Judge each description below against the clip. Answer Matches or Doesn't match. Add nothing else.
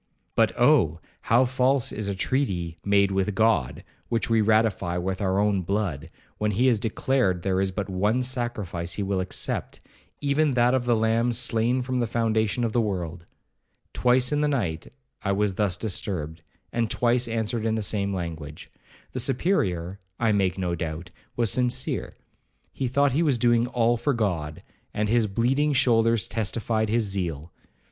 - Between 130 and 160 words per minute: Doesn't match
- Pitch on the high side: Doesn't match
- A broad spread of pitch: Doesn't match